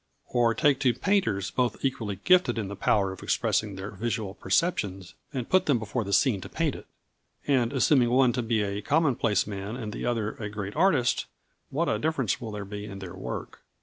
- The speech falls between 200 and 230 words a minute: Yes, fast, 205 wpm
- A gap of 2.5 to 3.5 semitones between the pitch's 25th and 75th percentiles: No, average, 4.6 semitones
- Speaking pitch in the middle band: No, low, 115 Hz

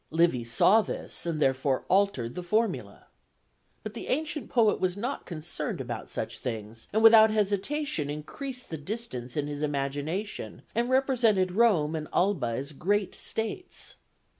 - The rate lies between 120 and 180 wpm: Yes, average, 145 wpm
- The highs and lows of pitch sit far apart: Yes, wide, 7.4 semitones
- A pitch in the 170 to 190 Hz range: Yes, medium, 185 Hz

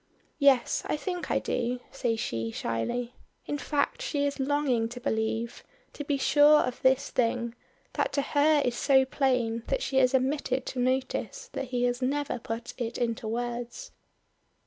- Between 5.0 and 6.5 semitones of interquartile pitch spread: No, average, 3.1 semitones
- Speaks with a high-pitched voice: Yes, very high, 255 Hz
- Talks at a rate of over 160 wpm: Yes, average, 170 wpm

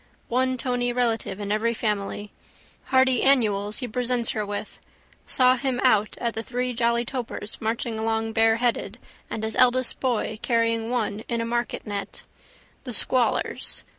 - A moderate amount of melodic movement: No, narrow, 2.1 semitones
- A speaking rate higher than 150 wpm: No, average, 145 wpm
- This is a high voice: Yes, high, 235 Hz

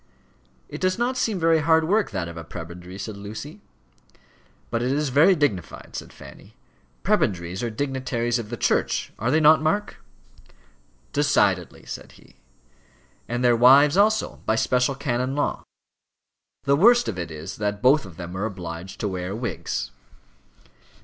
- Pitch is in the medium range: No, low, 120 Hz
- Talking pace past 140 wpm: Yes, average, 155 wpm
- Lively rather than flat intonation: Yes, wide, 7.8 semitones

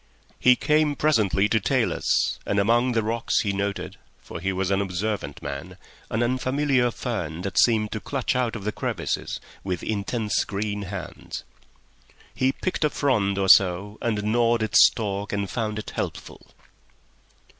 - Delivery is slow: No, average, 150 wpm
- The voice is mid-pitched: No, low, 105 Hz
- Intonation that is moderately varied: Yes, average, 3.3 semitones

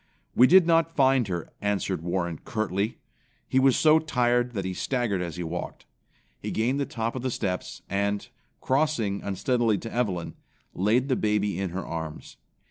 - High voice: No, low, 110 Hz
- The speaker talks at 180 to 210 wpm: No, average, 170 wpm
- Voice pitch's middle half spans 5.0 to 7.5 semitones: Yes, wide, 5.4 semitones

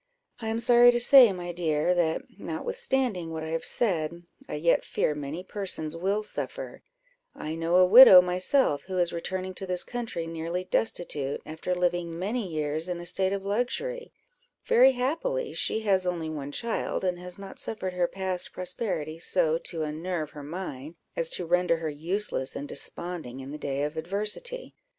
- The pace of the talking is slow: No, average, 175 wpm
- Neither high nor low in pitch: Yes, medium, 180 Hz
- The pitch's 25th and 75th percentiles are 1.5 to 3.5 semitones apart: No, average, 4.4 semitones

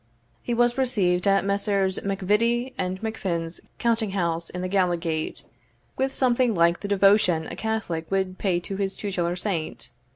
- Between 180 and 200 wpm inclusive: No, average, 155 wpm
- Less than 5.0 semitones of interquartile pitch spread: Yes, average, 3.8 semitones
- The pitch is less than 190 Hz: No, high, 195 Hz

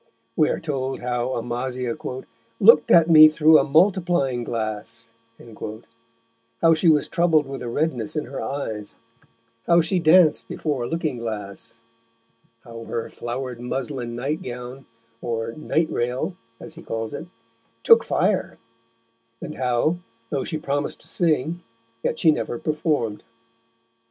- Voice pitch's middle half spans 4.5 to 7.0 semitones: Yes, average, 5.0 semitones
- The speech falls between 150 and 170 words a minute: No, slow, 135 wpm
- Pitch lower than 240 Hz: Yes, low, 135 Hz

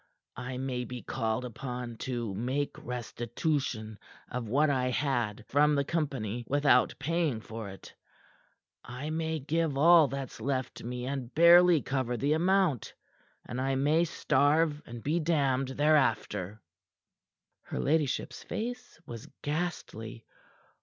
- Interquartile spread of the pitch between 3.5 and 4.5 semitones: Yes, average, 4.0 semitones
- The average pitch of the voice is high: No, low, 135 Hz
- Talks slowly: Yes, slow, 125 wpm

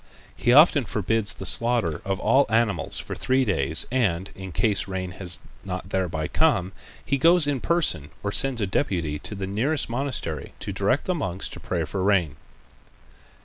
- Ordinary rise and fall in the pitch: No, wide, 6.0 semitones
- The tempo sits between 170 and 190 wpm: Yes, average, 175 wpm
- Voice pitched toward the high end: No, low, 100 Hz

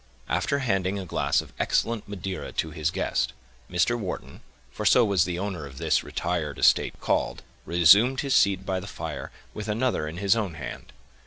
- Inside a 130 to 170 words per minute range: No, average, 180 wpm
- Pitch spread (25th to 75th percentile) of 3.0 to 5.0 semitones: Yes, average, 4.2 semitones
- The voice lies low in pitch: Yes, very low, 95 Hz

